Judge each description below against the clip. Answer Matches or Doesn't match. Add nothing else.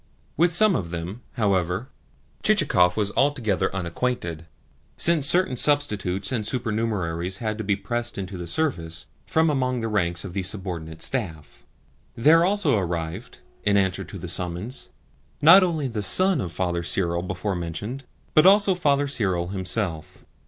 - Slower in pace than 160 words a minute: Matches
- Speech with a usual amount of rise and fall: Doesn't match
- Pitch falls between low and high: Doesn't match